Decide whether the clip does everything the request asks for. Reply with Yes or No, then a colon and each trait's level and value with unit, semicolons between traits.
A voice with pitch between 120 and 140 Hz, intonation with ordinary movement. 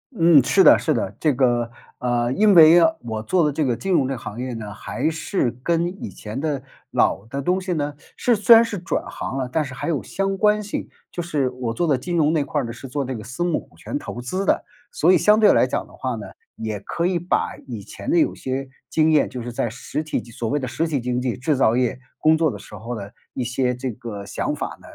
No: low, 135 Hz; wide, 5.7 semitones